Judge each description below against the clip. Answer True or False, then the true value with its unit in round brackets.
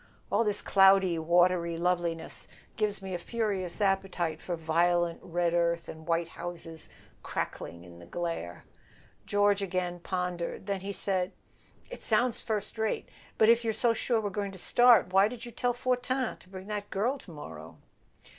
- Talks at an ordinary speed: True (170 wpm)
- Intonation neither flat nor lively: True (3.8 semitones)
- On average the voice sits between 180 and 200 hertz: True (185 Hz)